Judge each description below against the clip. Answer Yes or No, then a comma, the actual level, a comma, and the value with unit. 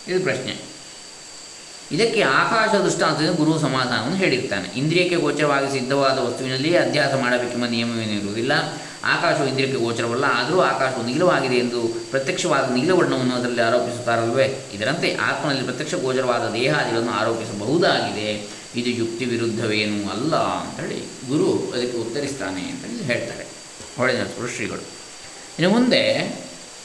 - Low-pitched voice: Yes, low, 125 Hz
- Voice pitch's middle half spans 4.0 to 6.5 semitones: No, average, 3.3 semitones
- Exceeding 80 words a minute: Yes, fast, 105 wpm